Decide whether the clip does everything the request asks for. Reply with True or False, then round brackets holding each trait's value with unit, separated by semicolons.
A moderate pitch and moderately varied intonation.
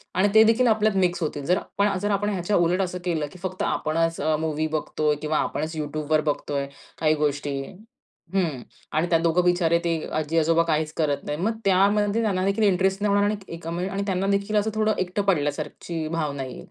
True (175 Hz; 4.2 semitones)